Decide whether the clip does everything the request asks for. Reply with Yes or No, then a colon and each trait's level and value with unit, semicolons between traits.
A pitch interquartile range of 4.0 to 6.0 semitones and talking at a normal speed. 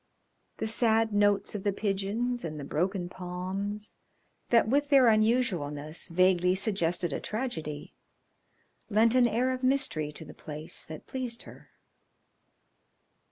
No: average, 5.0 semitones; slow, 130 wpm